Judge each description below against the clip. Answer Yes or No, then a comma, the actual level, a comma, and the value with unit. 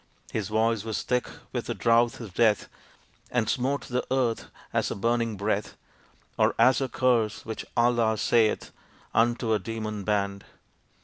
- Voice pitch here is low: Yes, low, 115 Hz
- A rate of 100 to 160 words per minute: Yes, average, 150 wpm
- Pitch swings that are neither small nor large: No, narrow, 1.9 semitones